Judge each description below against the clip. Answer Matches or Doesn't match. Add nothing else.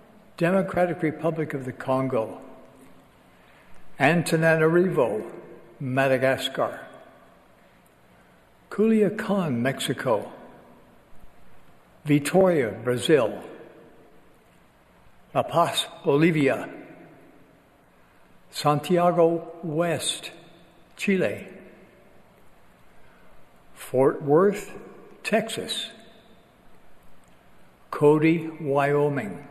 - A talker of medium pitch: Matches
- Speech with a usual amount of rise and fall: Matches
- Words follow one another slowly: Matches